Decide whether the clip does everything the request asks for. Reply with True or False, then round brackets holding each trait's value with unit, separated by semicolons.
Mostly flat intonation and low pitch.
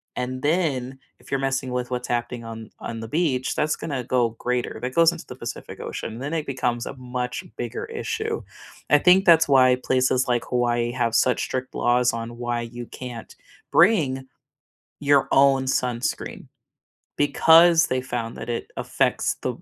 False (3.1 semitones; 130 Hz)